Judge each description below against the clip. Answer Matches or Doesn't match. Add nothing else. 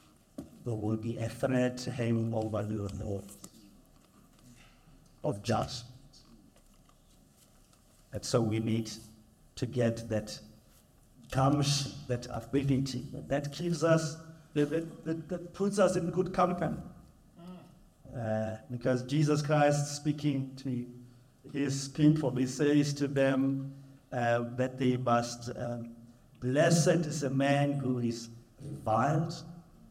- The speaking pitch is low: Matches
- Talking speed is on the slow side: Matches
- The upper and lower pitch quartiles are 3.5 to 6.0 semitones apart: Matches